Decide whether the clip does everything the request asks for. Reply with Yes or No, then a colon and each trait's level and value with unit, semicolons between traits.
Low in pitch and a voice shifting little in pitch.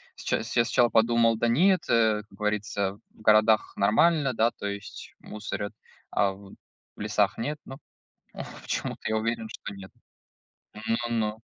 Yes: low, 110 Hz; narrow, 2.0 semitones